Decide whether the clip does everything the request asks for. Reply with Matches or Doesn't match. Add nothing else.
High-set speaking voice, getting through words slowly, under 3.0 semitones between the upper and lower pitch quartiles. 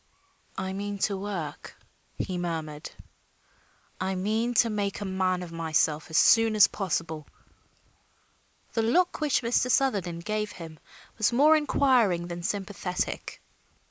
Doesn't match